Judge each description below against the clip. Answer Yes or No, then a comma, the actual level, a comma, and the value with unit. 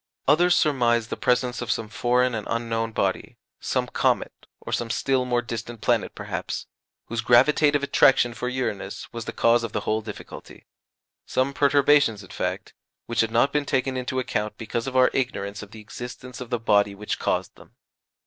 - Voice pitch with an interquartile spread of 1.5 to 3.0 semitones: Yes, narrow, 2.4 semitones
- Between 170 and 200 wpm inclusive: Yes, average, 180 wpm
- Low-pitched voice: Yes, low, 120 Hz